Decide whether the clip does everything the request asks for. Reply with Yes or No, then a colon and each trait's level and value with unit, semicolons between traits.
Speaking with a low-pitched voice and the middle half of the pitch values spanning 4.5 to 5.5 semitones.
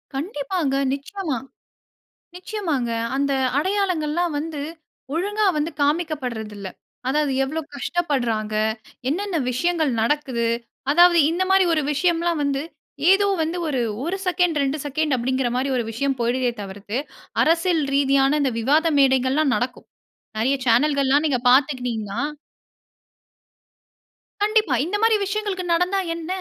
No: very high, 295 Hz; average, 4.9 semitones